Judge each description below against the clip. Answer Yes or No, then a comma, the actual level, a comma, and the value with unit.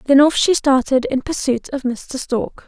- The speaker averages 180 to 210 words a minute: Yes, average, 200 wpm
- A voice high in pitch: Yes, very high, 275 Hz